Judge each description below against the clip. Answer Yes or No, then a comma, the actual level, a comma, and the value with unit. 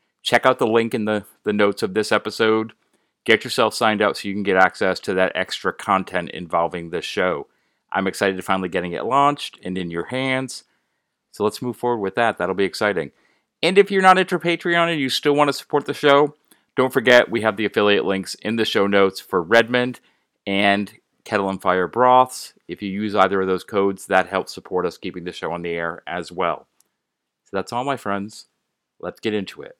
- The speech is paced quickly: Yes, fast, 215 wpm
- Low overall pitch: Yes, low, 105 Hz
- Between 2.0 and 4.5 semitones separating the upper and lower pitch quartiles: No, average, 5.1 semitones